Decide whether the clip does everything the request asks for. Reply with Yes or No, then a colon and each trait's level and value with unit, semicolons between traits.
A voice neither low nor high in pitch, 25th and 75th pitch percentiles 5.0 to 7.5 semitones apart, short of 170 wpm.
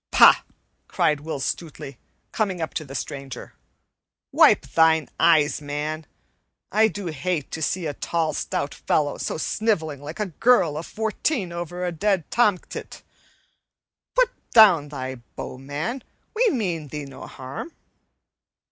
Yes: medium, 160 Hz; average, 5.3 semitones; average, 140 wpm